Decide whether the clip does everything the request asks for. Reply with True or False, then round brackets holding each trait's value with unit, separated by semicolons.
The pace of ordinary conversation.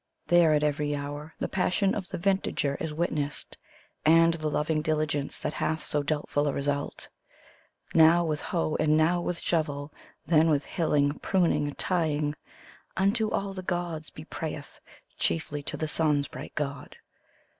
True (155 wpm)